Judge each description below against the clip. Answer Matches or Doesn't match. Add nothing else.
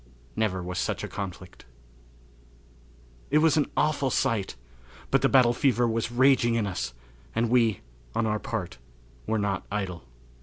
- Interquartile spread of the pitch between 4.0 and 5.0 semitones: Matches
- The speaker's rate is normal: Matches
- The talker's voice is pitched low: Matches